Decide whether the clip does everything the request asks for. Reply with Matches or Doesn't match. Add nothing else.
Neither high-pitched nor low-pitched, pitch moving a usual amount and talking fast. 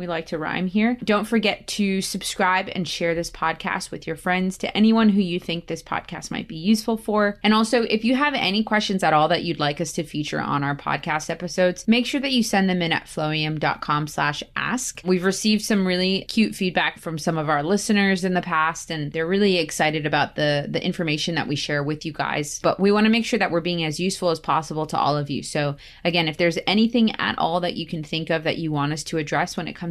Matches